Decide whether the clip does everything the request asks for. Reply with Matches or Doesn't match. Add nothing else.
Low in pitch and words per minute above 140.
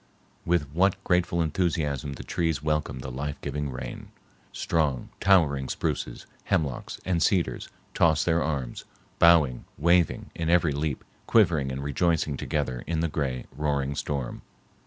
Doesn't match